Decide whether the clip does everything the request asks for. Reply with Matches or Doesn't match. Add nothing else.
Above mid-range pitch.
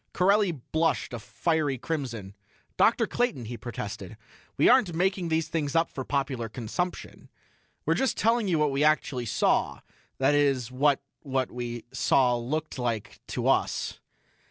Doesn't match